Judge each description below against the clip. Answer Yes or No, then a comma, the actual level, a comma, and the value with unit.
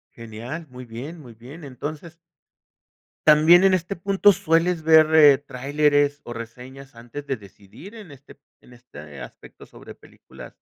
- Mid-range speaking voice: Yes, medium, 145 Hz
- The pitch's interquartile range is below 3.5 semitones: No, average, 4.9 semitones